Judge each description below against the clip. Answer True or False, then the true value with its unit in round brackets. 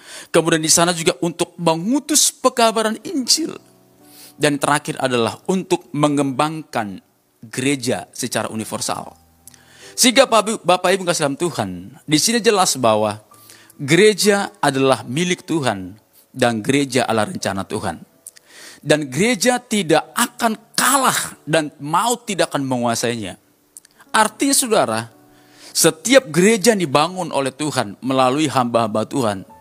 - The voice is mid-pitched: True (155 Hz)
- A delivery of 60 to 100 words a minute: False (115 wpm)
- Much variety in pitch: True (8.5 semitones)